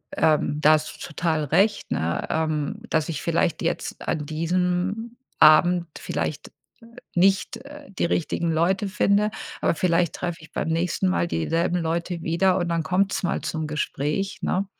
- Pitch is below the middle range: No, medium, 170 Hz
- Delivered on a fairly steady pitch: No, average, 3.0 semitones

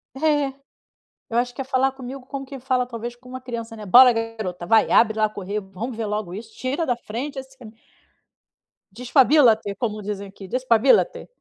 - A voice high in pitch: Yes, high, 240 Hz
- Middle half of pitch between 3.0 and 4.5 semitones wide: Yes, average, 3.4 semitones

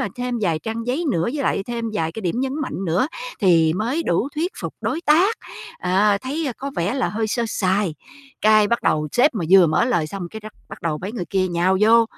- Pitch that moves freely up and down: Yes, wide, 5.8 semitones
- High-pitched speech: Yes, high, 215 Hz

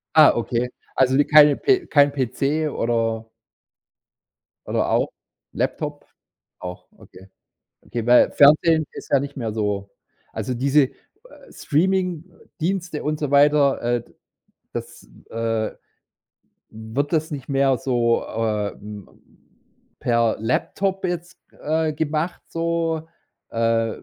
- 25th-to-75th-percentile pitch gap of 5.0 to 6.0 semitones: Yes, wide, 5.5 semitones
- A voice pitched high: No, medium, 140 Hz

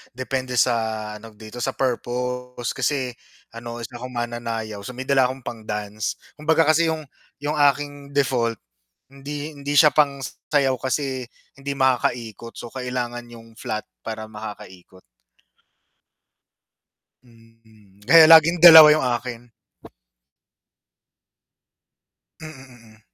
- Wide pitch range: No, average, 3.5 semitones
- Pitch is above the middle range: No, low, 125 Hz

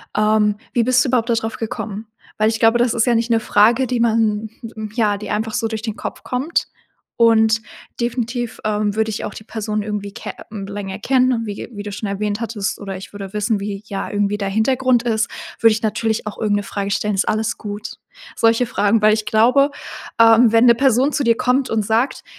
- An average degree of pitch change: No, narrow, 2.0 semitones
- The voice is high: Yes, high, 220 Hz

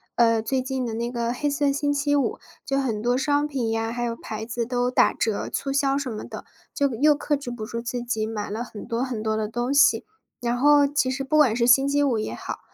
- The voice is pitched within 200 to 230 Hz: No, high, 245 Hz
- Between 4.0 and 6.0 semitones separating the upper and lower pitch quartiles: No, average, 3.4 semitones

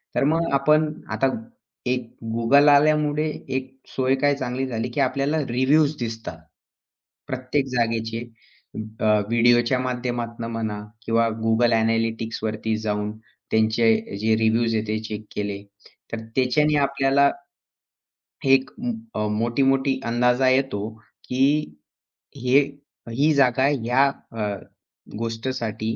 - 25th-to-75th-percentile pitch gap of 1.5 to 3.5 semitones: Yes, average, 3.2 semitones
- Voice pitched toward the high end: No, low, 120 Hz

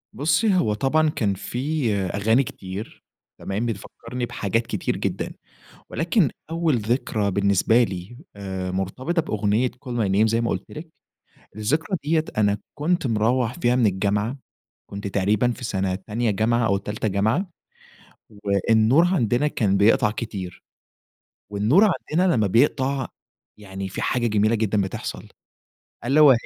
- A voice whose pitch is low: Yes, low, 115 Hz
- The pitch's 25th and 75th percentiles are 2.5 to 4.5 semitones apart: No, average, 4.9 semitones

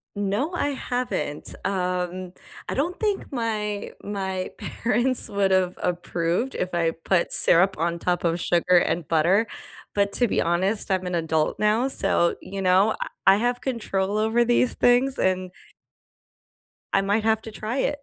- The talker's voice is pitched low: No, high, 195 Hz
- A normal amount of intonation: Yes, average, 4.3 semitones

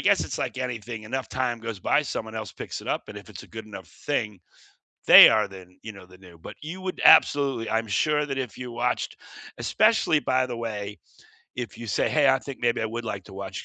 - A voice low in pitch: Yes, low, 115 Hz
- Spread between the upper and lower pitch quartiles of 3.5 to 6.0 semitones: Yes, average, 3.9 semitones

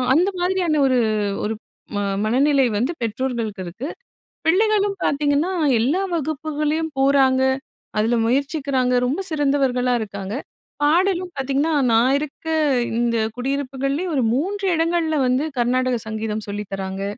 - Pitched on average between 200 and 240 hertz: No, very high, 275 Hz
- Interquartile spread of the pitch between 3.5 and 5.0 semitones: Yes, average, 4.5 semitones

